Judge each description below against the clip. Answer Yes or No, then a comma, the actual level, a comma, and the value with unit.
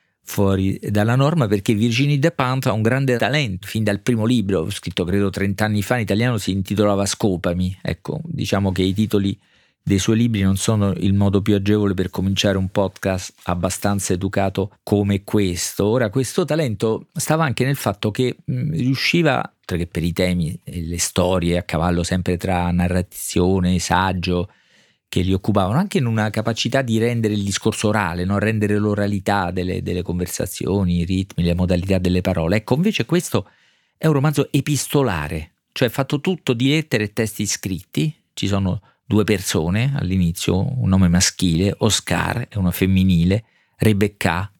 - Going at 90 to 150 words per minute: No, average, 165 wpm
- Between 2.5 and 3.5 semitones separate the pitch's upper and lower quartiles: No, average, 4.1 semitones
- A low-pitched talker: Yes, low, 100 Hz